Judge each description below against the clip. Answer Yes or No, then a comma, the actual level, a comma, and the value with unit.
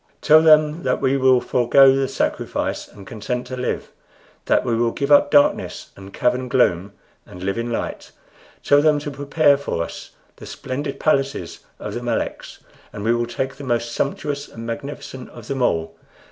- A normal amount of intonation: Yes, average, 3.4 semitones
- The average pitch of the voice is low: Yes, low, 130 Hz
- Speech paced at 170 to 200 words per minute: Yes, average, 180 wpm